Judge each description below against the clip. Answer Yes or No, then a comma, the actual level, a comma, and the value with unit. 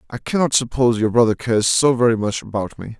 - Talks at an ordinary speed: No, fast, 220 wpm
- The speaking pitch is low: Yes, low, 115 Hz